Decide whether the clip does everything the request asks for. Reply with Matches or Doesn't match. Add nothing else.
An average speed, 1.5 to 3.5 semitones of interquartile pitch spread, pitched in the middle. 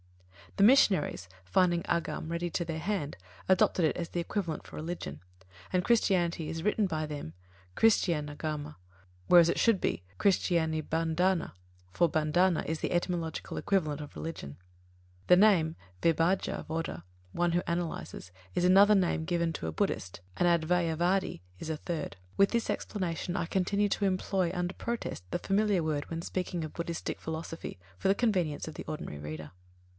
Matches